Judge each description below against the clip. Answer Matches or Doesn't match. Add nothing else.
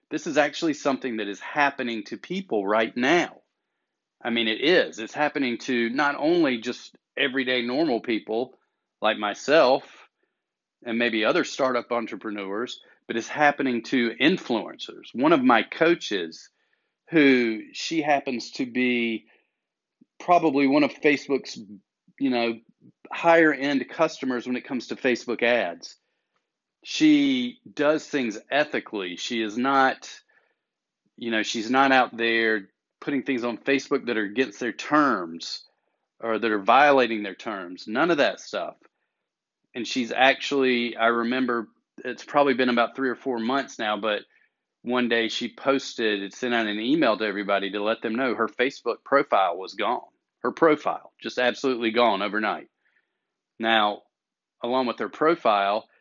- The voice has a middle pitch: Doesn't match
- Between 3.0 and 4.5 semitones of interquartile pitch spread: Matches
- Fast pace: Doesn't match